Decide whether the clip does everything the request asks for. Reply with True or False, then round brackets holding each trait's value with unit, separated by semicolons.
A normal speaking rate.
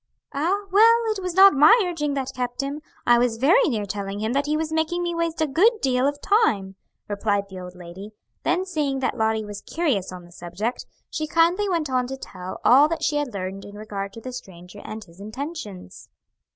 False (215 wpm)